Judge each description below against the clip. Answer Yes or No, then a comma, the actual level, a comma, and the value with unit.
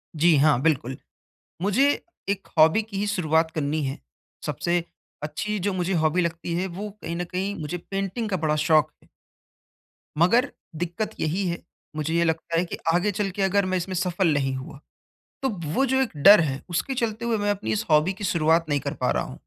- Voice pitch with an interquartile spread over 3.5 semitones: Yes, average, 4.3 semitones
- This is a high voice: No, medium, 175 Hz